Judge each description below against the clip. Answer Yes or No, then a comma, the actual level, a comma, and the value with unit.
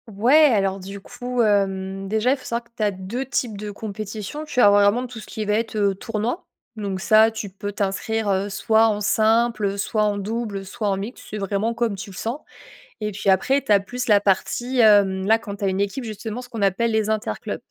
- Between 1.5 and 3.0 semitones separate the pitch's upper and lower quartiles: Yes, narrow, 2.6 semitones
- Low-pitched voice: No, high, 210 Hz